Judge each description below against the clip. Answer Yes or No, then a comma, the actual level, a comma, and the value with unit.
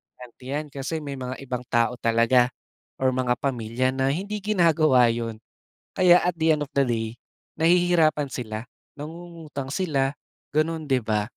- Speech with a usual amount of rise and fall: Yes, average, 4.5 semitones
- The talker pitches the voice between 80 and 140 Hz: Yes, low, 135 Hz